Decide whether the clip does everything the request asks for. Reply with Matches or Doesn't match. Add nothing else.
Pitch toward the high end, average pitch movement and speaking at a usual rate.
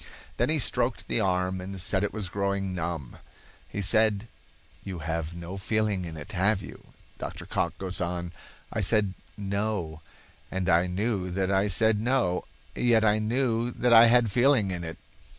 Doesn't match